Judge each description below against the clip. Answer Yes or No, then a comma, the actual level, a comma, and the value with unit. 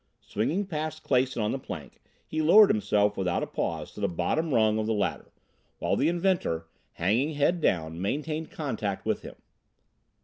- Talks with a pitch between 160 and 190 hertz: No, low, 130 Hz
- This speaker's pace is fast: No, average, 170 wpm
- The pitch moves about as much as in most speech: No, wide, 7.5 semitones